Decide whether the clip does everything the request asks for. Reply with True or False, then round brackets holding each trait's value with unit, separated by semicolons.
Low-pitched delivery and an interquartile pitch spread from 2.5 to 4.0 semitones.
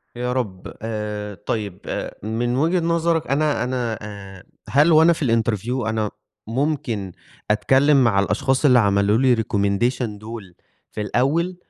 False (120 Hz; 4.5 semitones)